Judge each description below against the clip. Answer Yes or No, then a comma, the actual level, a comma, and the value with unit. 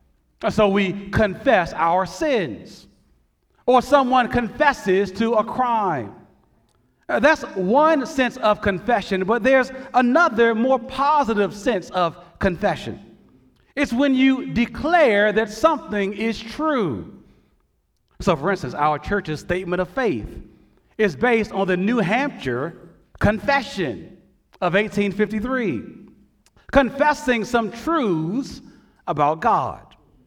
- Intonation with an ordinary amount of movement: Yes, average, 4.8 semitones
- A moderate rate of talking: No, slow, 105 wpm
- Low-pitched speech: No, high, 230 Hz